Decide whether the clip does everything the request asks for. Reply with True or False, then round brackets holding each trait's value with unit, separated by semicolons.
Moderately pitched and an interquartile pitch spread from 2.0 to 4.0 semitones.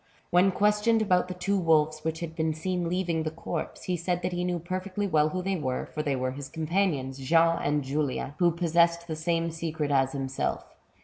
True (165 Hz; 2.8 semitones)